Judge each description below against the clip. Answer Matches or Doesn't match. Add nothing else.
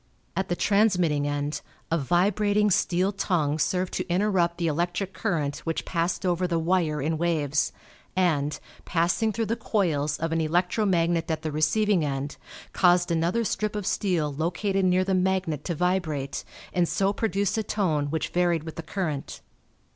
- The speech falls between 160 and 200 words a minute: Matches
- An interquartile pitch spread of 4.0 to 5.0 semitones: Doesn't match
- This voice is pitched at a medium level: Matches